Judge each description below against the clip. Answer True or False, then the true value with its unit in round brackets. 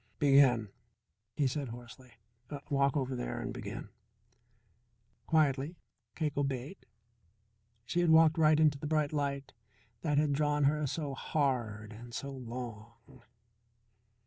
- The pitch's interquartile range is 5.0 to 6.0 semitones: False (3.3 semitones)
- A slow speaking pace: True (120 wpm)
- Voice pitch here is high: False (140 Hz)